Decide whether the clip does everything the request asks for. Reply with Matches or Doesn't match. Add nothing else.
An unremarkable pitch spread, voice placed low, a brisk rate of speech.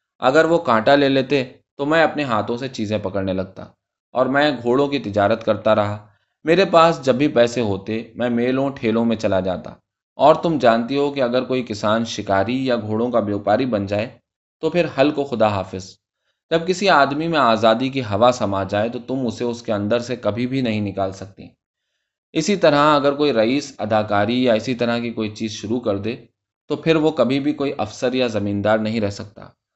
Matches